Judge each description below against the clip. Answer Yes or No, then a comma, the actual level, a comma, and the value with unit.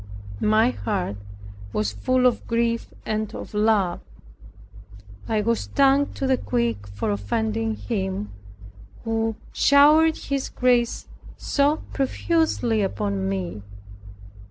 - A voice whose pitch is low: No, high, 220 Hz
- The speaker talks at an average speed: No, slow, 110 wpm